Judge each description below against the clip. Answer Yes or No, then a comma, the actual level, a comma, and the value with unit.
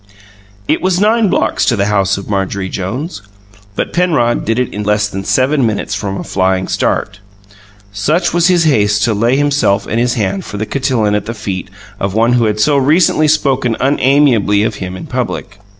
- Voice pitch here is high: No, low, 110 Hz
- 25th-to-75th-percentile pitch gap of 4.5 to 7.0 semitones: Yes, wide, 5.6 semitones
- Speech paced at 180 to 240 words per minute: Yes, average, 195 wpm